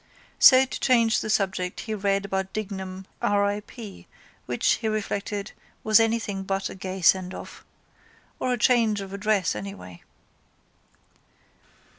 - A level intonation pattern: Yes, narrow, 2.3 semitones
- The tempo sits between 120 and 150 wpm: Yes, slow, 135 wpm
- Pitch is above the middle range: Yes, high, 200 Hz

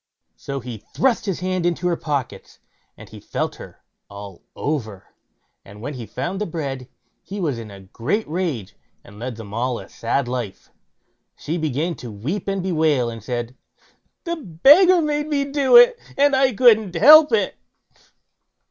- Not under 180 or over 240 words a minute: No, average, 165 wpm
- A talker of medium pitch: Yes, medium, 160 Hz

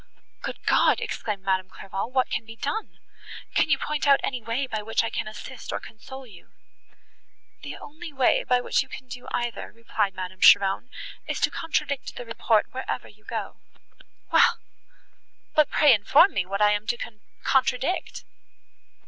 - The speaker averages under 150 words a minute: No, average, 165 wpm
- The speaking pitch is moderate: No, high, 235 Hz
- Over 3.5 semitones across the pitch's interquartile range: Yes, average, 4.3 semitones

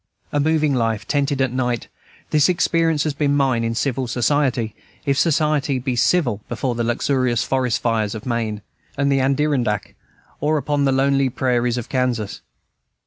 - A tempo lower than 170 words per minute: Yes, average, 160 wpm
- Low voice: Yes, low, 130 Hz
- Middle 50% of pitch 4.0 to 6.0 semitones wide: No, average, 3.3 semitones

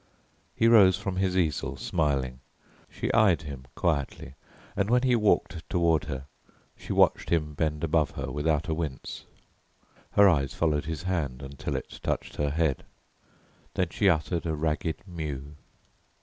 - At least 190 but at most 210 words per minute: No, average, 150 wpm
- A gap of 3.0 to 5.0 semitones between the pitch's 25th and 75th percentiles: Yes, average, 3.8 semitones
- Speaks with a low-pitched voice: Yes, very low, 80 Hz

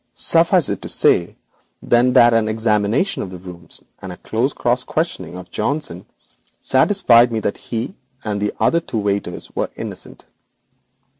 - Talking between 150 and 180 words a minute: No, average, 140 wpm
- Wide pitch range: No, average, 3.9 semitones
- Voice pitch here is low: Yes, low, 115 Hz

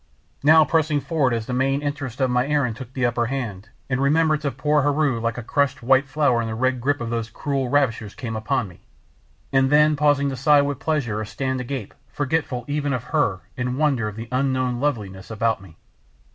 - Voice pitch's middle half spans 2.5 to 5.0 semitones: Yes, average, 3.6 semitones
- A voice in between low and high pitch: No, low, 130 Hz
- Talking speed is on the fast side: Yes, fast, 210 wpm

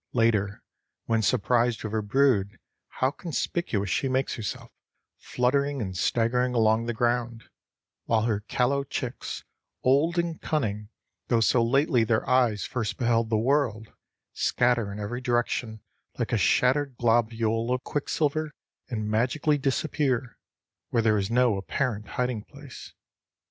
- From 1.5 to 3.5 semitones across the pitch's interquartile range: Yes, average, 3.1 semitones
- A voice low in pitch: Yes, low, 120 Hz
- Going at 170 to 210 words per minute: No, slow, 135 wpm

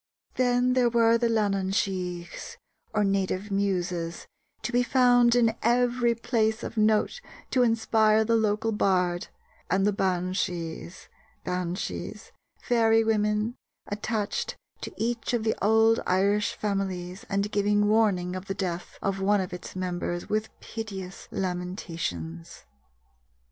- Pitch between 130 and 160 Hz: No, high, 205 Hz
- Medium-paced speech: No, slow, 130 wpm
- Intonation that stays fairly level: No, average, 3.5 semitones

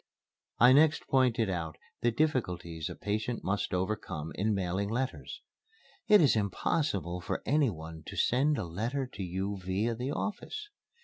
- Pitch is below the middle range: Yes, low, 105 Hz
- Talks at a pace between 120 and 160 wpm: Yes, average, 150 wpm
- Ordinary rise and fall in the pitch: No, wide, 6.4 semitones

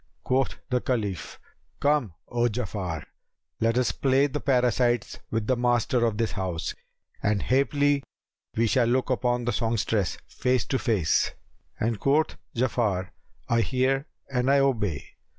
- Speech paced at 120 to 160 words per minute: Yes, average, 140 wpm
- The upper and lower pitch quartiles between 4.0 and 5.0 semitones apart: No, average, 3.2 semitones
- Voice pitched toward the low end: Yes, low, 120 Hz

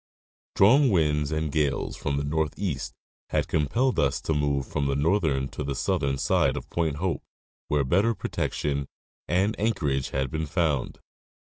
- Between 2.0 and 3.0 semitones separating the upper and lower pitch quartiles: No, average, 4.2 semitones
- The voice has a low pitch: Yes, very low, 75 Hz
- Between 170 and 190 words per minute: No, average, 155 wpm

